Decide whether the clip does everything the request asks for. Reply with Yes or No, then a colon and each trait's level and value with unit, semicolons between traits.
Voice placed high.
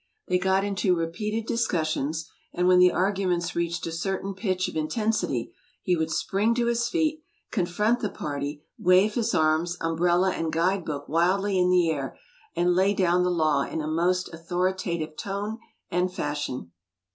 No: medium, 180 Hz